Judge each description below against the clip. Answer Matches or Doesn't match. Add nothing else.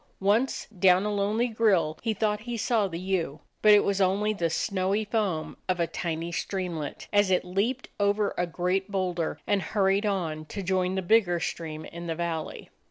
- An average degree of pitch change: Matches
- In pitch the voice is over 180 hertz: Matches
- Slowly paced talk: Doesn't match